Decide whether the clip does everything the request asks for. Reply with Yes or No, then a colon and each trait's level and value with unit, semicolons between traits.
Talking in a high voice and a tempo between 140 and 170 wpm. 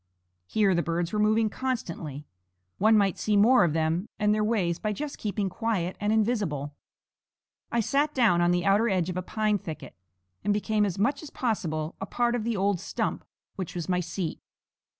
No: high, 205 Hz; average, 190 wpm